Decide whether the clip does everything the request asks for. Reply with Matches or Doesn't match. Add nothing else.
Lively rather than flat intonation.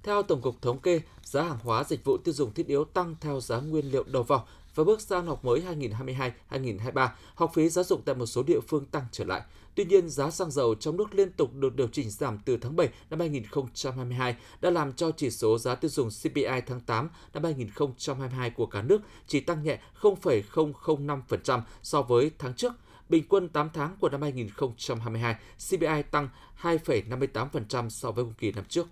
Doesn't match